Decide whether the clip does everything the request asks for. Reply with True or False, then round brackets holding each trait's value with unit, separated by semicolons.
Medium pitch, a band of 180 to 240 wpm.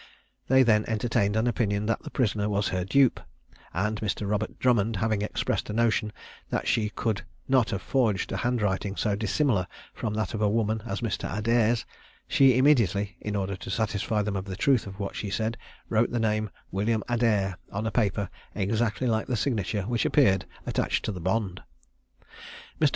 False (110 Hz; 185 wpm)